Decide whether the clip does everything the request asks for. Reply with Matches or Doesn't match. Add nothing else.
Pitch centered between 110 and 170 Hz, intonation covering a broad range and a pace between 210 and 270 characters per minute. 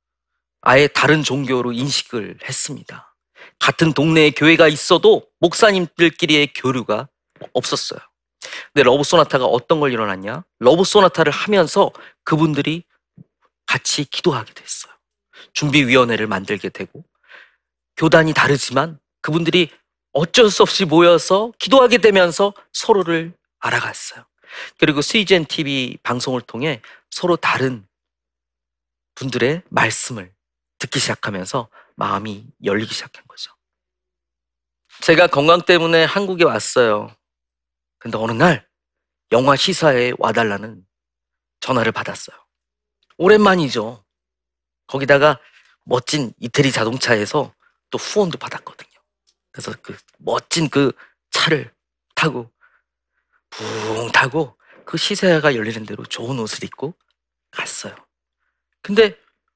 Matches